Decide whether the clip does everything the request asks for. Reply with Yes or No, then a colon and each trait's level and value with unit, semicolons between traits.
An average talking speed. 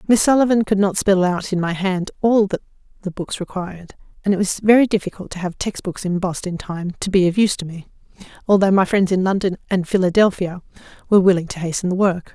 No: fast, 215 wpm